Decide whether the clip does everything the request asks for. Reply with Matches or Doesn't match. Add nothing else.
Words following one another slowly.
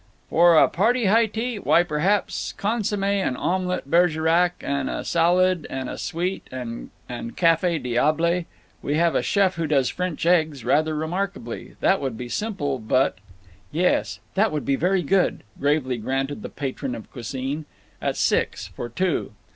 Doesn't match